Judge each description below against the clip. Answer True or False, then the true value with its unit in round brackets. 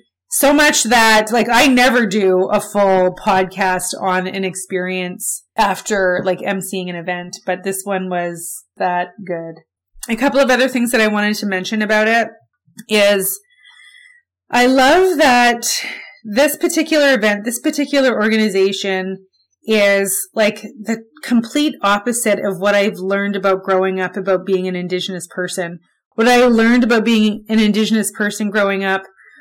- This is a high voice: True (210 Hz)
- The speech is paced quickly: False (150 wpm)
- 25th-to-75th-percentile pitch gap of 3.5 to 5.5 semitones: True (4.2 semitones)